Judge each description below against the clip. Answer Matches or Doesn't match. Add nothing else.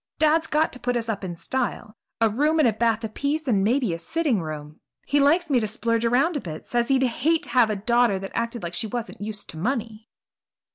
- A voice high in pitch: Matches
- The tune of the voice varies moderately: Matches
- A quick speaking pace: Matches